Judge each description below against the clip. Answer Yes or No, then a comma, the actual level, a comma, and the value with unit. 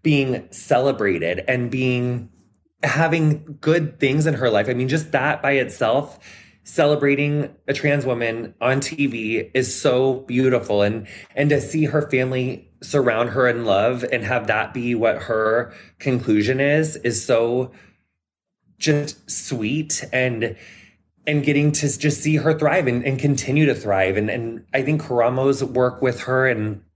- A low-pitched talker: Yes, low, 130 Hz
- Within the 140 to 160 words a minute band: Yes, average, 155 wpm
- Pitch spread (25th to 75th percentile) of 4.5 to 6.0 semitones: No, average, 4.1 semitones